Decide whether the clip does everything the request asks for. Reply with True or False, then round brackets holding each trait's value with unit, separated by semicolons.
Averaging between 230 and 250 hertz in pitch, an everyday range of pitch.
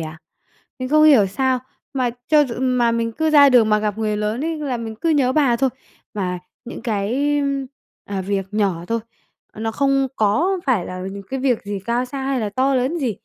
True (245 Hz; 4.5 semitones)